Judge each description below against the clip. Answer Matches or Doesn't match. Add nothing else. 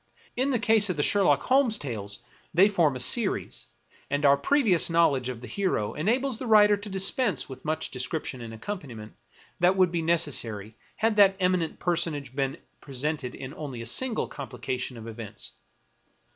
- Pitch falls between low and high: Matches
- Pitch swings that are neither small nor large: Doesn't match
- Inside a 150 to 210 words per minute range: Matches